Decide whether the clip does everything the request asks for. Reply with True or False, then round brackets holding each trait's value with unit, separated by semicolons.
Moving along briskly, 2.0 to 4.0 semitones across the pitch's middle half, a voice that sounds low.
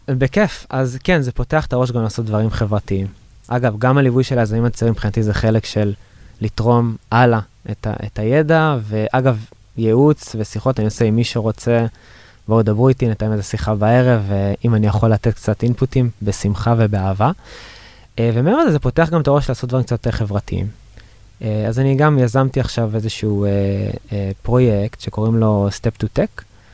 True (165 wpm; 3.0 semitones; 115 Hz)